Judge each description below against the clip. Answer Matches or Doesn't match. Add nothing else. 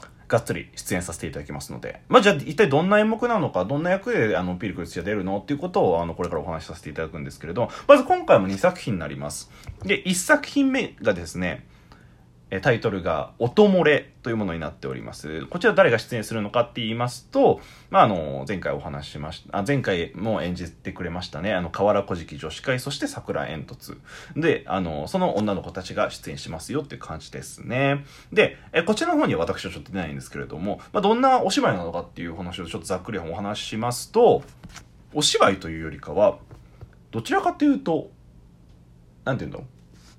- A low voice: Matches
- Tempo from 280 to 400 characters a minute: Doesn't match